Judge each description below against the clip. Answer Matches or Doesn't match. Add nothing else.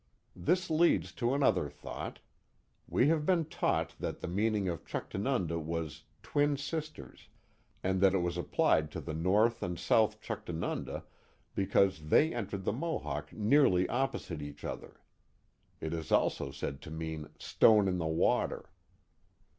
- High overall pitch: Doesn't match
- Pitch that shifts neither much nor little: Doesn't match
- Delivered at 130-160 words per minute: Matches